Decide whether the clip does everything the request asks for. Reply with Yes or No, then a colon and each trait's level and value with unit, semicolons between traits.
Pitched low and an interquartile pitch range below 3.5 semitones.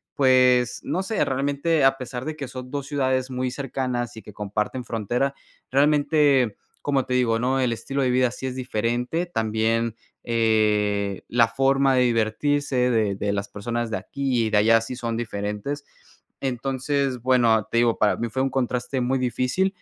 Yes: low, 125 Hz; average, 2.9 semitones